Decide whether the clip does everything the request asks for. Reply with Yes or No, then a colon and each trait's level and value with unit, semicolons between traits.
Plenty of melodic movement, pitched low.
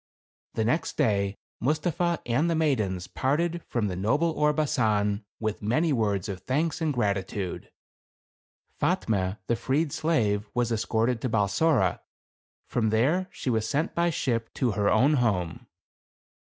Yes: wide, 6.5 semitones; low, 120 Hz